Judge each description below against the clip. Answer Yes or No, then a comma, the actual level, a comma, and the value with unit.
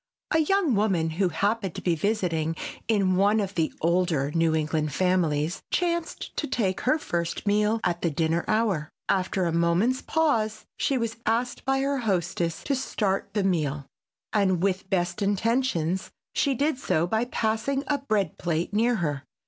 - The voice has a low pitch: No, high, 195 Hz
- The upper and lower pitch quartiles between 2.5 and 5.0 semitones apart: No, wide, 5.4 semitones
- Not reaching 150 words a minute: No, average, 165 wpm